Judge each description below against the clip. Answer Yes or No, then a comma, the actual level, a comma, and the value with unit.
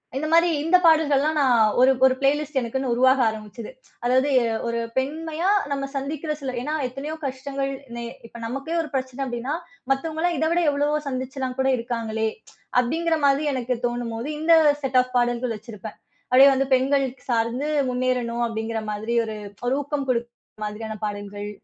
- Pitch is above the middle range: Yes, very high, 260 Hz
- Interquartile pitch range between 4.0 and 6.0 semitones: No, average, 3.2 semitones